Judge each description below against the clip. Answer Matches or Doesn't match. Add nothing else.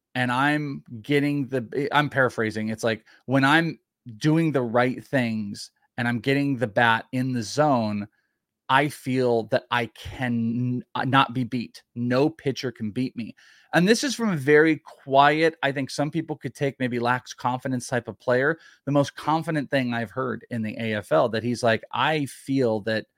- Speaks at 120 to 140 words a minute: Doesn't match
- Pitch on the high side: Doesn't match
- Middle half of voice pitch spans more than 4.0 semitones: Doesn't match